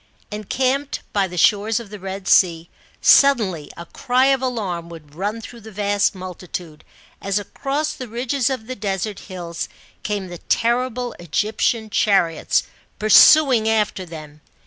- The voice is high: Yes, high, 210 Hz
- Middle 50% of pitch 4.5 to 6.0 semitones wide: Yes, average, 5.0 semitones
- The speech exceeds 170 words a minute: No, average, 145 wpm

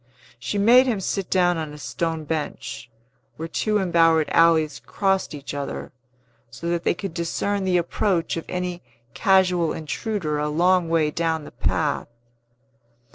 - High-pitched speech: No, medium, 170 Hz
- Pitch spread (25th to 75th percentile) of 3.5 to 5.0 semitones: No, average, 3.1 semitones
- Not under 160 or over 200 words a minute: No, average, 150 wpm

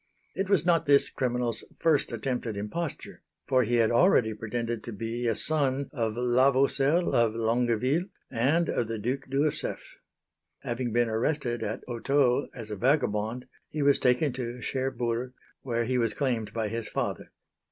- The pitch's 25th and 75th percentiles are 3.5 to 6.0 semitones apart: No, average, 3.1 semitones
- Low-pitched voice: Yes, low, 125 Hz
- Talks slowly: No, average, 165 wpm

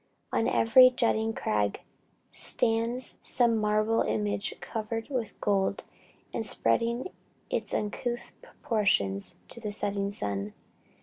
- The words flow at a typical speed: No, slow, 110 wpm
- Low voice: No, high, 220 Hz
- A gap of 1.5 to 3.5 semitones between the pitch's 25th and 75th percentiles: Yes, narrow, 2.6 semitones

